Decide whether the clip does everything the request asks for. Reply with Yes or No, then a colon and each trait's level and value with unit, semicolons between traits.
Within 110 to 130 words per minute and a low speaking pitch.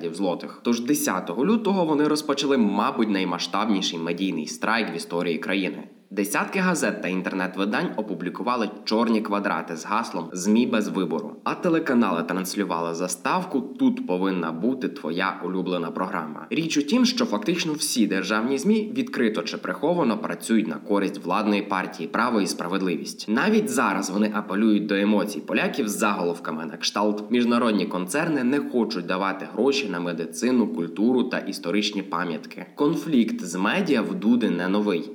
No: average, 145 wpm; low, 105 Hz